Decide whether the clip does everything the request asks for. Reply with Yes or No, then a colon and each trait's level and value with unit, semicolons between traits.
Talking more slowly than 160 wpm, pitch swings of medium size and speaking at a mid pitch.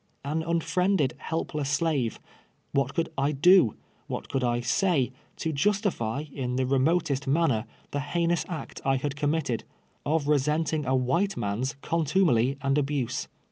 Yes: average, 145 wpm; average, 3.8 semitones; medium, 145 Hz